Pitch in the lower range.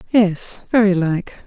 No: high, 195 Hz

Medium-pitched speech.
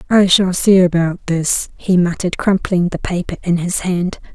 Yes: medium, 180 Hz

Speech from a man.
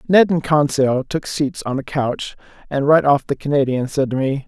Yes: male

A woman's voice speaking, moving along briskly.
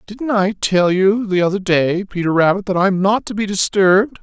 No: male; fast, 215 wpm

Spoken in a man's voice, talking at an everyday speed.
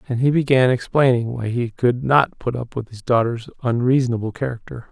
Yes: male; average, 185 wpm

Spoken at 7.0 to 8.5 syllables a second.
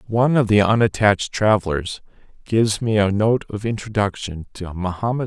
No: 5.5 syllables/s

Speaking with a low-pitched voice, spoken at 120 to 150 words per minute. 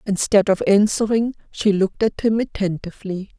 No: high, 205 Hz; average, 140 wpm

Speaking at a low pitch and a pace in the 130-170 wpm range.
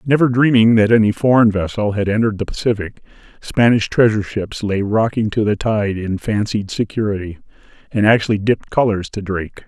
Yes: low, 105 Hz; average, 165 wpm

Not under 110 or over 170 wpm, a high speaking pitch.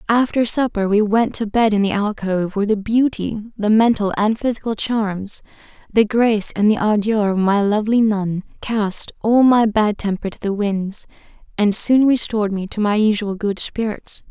No: average, 180 wpm; high, 210 Hz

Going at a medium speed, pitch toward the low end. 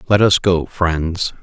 Yes: average, 170 wpm; very low, 90 Hz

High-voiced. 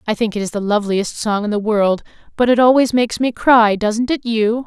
Yes: high, 220 Hz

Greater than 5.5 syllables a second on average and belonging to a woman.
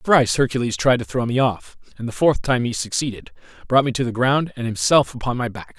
No: 5.9 syllables/s; male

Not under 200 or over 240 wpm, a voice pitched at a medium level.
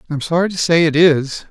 No: fast, 280 wpm; medium, 160 Hz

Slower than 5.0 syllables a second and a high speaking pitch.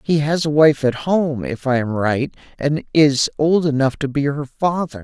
No: 4.4 syllables/s; medium, 145 Hz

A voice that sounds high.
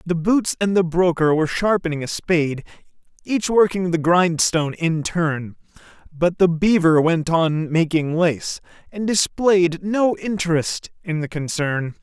No: medium, 170 Hz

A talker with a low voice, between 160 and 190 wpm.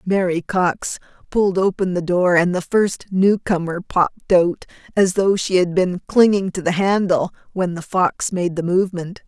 No: medium, 185 Hz; average, 175 wpm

